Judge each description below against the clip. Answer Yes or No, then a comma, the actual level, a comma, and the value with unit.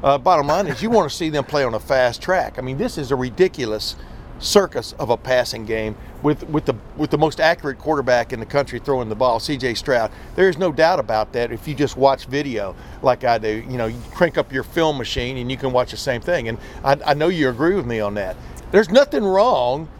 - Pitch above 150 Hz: No, low, 135 Hz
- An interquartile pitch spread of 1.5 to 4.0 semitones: No, average, 4.6 semitones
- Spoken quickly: Yes, fast, 250 wpm